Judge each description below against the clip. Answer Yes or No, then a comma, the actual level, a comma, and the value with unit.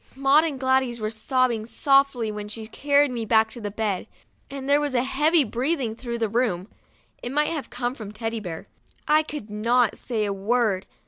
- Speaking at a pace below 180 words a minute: No, average, 190 wpm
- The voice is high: Yes, high, 240 Hz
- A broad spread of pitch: No, average, 3.9 semitones